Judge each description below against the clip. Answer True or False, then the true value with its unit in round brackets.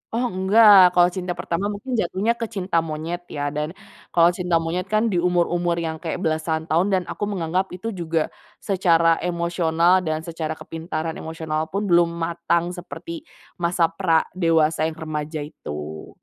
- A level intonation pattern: True (2.3 semitones)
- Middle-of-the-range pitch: True (170 Hz)